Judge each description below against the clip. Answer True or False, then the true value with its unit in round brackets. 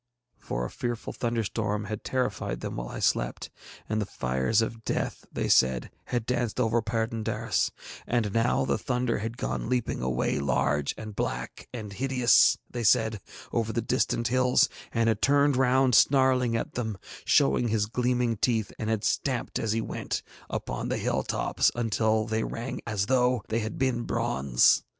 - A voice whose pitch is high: False (115 Hz)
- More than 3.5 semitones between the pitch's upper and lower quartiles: False (2.7 semitones)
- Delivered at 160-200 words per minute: True (170 wpm)